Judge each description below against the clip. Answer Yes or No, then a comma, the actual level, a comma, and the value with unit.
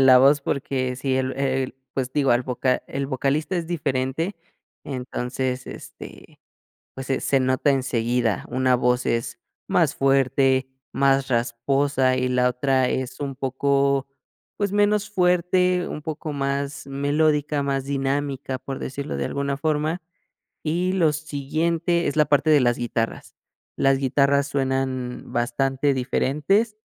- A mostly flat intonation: Yes, narrow, 2.3 semitones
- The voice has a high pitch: No, low, 135 Hz